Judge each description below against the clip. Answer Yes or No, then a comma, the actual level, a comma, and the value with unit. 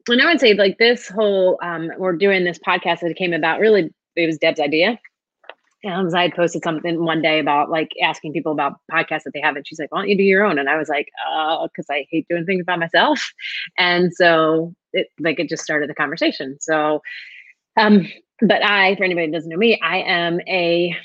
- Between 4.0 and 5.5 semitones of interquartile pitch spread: No, average, 3.4 semitones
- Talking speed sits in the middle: No, fast, 230 wpm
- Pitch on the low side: No, medium, 170 Hz